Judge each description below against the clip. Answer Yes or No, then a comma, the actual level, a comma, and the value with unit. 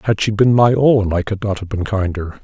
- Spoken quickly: Yes, fast, 270 wpm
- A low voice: Yes, low, 105 Hz